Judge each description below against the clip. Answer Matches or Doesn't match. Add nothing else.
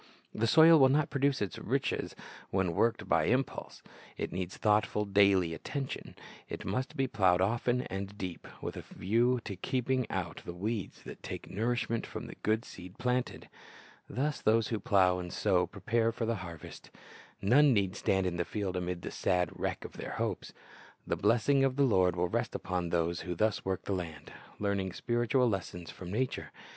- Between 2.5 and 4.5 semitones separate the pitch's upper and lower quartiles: Doesn't match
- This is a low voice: Matches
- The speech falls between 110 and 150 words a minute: Doesn't match